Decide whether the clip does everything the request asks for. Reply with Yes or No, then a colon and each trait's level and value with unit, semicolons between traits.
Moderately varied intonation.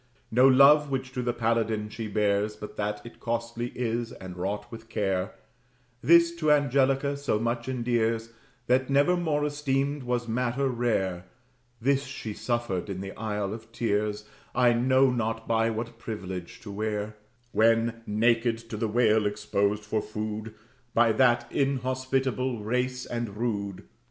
Yes: average, 3.3 semitones